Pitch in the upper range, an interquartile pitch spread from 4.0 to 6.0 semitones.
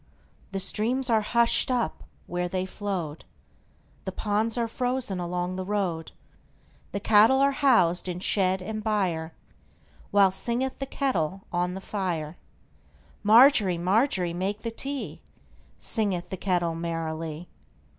Yes: high, 195 Hz; average, 4.4 semitones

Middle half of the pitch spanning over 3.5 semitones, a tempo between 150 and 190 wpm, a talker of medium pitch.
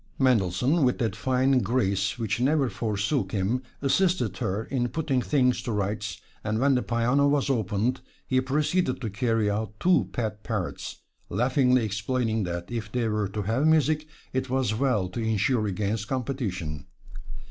No: average, 4.1 semitones; average, 160 wpm; low, 120 Hz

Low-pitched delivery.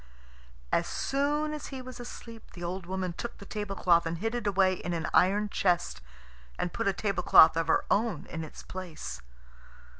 No: high, 190 Hz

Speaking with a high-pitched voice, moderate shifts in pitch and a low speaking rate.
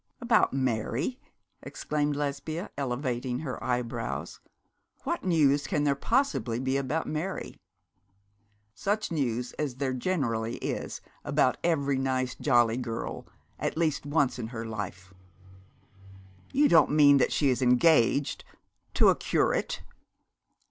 No: low, 135 Hz; average, 3.8 semitones; slow, 120 wpm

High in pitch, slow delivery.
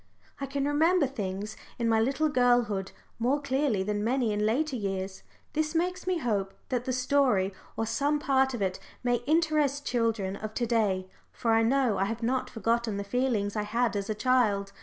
No: high, 235 Hz; average, 190 wpm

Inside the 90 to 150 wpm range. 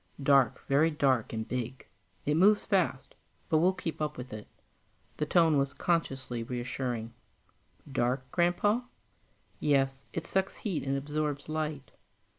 Yes: slow, 135 wpm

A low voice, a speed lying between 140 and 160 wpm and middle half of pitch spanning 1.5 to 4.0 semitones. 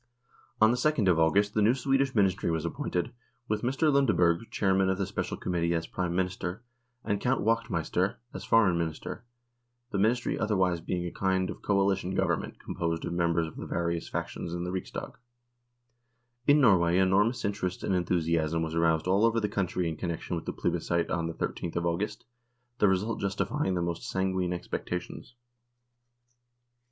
No: very low, 95 Hz; average, 170 wpm; average, 3.6 semitones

